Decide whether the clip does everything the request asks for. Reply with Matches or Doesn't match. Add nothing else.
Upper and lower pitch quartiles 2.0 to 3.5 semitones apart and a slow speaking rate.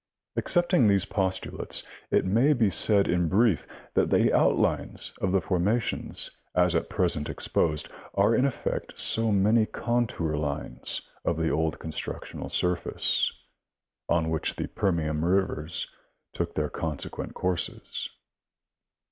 Doesn't match